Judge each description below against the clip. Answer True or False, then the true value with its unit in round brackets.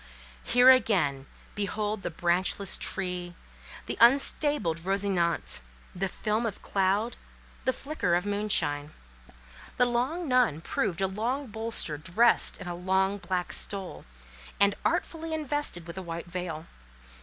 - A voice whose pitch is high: True (195 Hz)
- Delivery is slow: True (125 wpm)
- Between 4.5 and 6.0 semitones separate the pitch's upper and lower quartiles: True (5.3 semitones)